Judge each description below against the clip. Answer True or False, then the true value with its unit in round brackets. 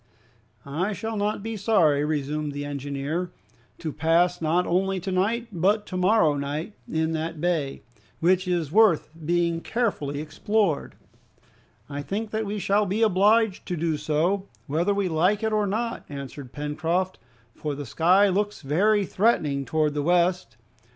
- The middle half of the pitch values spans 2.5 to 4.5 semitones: False (5.1 semitones)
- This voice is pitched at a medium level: True (175 Hz)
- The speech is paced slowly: False (150 wpm)